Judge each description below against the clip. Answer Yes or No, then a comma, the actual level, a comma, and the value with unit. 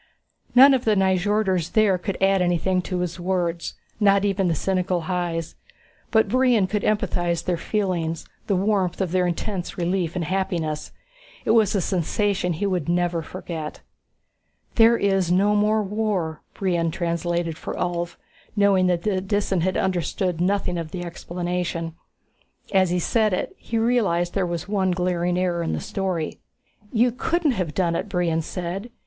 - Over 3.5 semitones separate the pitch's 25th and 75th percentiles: No, average, 2.7 semitones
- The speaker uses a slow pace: No, average, 165 wpm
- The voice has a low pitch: No, medium, 185 Hz